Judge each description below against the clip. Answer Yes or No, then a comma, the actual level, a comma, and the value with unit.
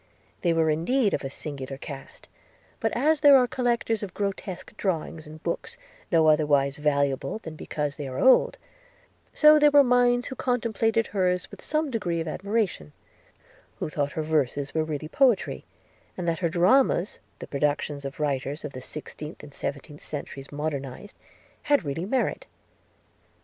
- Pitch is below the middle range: No, medium, 160 Hz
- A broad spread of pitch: Yes, wide, 7.7 semitones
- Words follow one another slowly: No, average, 160 wpm